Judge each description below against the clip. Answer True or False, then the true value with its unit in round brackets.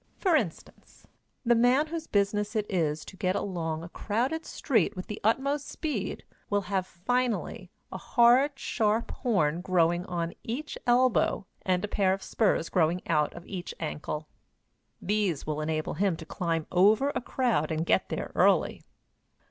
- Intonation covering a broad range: True (6.0 semitones)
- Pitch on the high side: True (200 Hz)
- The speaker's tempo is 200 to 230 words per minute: False (160 wpm)